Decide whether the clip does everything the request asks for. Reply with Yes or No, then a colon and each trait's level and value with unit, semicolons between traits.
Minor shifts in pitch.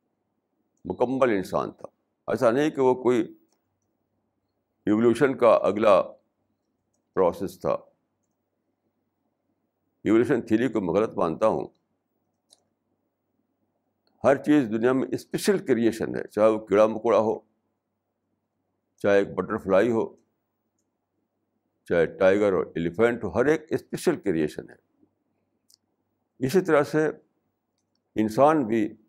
No: average, 3.3 semitones